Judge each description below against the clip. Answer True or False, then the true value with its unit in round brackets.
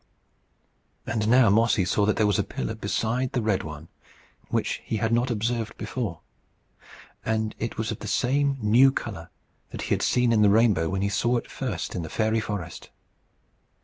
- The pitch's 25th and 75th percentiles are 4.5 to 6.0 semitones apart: False (2.7 semitones)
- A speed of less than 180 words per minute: False (185 wpm)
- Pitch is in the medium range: False (110 Hz)